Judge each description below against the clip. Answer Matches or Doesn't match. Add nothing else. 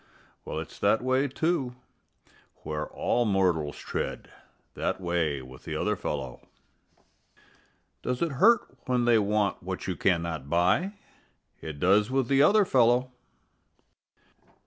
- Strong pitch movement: Matches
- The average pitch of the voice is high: Doesn't match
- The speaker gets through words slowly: Matches